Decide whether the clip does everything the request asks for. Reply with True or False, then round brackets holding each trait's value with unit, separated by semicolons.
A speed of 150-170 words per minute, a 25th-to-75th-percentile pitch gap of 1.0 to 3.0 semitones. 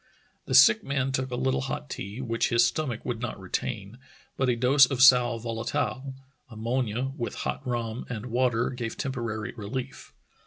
True (165 wpm; 2.4 semitones)